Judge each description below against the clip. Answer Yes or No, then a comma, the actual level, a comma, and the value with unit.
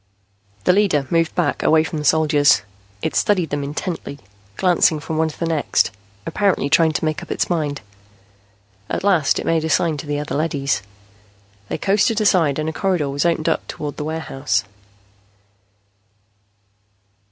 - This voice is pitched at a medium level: Yes, medium, 160 Hz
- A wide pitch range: No, average, 2.8 semitones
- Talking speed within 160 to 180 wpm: Yes, average, 165 wpm